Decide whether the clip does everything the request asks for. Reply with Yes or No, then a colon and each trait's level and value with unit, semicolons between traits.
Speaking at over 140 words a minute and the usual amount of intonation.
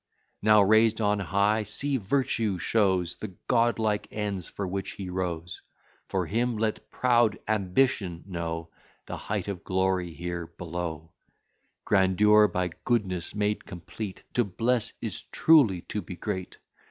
No: slow, 135 wpm; average, 3.3 semitones